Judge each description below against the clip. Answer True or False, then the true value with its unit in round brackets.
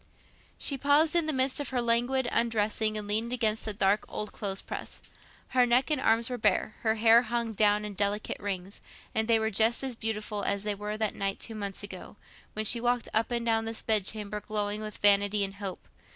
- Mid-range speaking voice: False (220 Hz)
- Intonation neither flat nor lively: False (2.3 semitones)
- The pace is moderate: False (210 wpm)